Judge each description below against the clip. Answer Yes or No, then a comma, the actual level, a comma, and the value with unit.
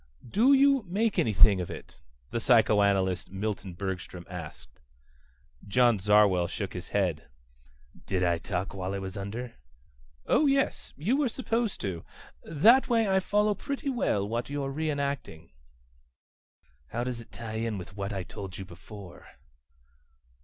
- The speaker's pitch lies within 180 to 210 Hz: No, low, 105 Hz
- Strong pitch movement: Yes, wide, 8.9 semitones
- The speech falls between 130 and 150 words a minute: Yes, average, 145 wpm